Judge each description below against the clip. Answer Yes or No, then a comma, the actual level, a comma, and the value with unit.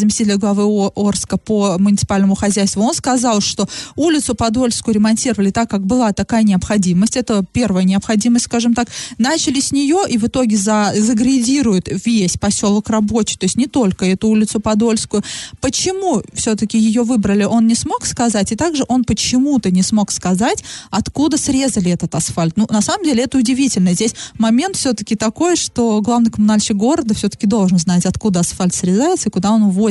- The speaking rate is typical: No, fast, 165 wpm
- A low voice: No, high, 220 Hz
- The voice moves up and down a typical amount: Yes, average, 3.4 semitones